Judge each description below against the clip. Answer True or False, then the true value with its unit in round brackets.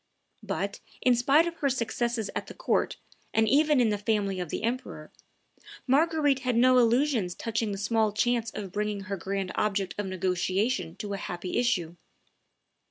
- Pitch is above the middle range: True (220 Hz)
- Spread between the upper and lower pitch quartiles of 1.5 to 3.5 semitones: False (4.2 semitones)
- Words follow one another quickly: False (165 wpm)